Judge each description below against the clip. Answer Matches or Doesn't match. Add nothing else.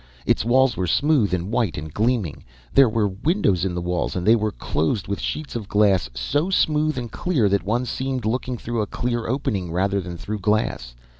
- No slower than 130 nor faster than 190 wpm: Doesn't match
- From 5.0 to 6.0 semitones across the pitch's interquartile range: Matches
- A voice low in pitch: Matches